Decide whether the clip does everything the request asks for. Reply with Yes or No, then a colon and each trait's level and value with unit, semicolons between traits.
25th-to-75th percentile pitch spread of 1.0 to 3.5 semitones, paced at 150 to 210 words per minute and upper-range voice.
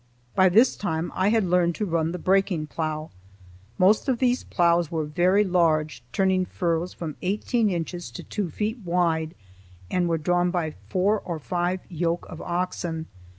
No: narrow, 2.5 semitones; average, 165 wpm; medium, 175 Hz